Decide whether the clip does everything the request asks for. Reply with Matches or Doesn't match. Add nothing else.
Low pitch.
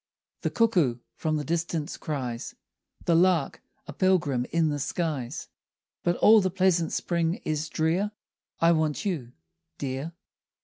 Doesn't match